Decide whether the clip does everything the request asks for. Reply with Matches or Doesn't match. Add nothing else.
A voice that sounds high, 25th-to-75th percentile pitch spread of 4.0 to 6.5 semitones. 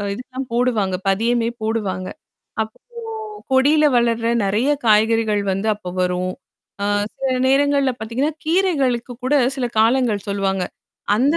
Matches